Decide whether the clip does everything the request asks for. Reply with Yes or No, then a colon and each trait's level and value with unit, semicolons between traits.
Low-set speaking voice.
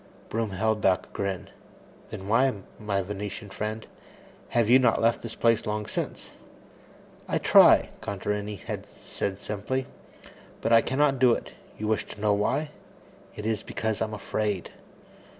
Yes: low, 105 Hz